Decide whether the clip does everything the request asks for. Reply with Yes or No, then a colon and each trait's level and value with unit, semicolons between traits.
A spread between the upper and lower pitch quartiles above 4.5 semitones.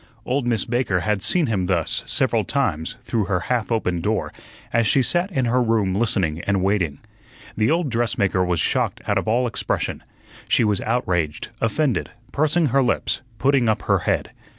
Yes: average, 5.0 semitones